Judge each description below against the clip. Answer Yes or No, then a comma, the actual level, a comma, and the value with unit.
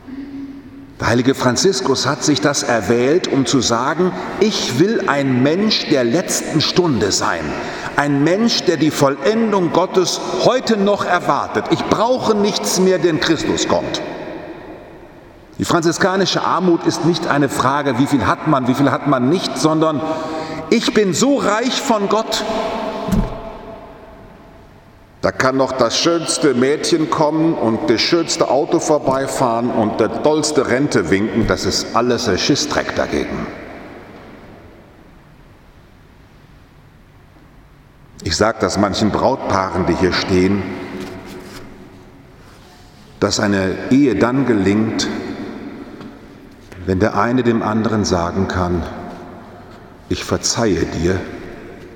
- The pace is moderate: No, slow, 120 wpm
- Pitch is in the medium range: Yes, medium, 145 Hz